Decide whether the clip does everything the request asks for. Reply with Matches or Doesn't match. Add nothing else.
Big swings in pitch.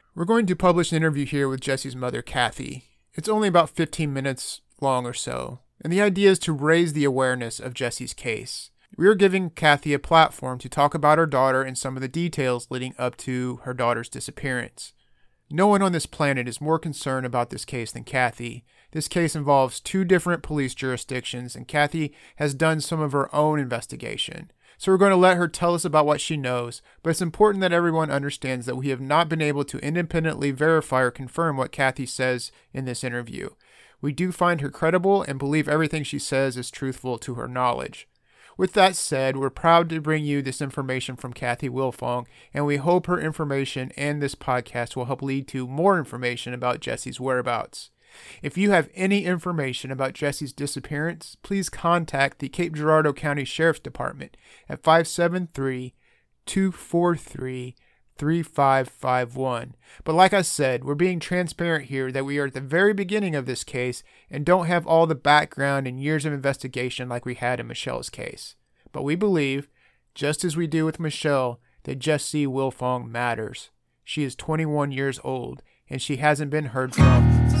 Doesn't match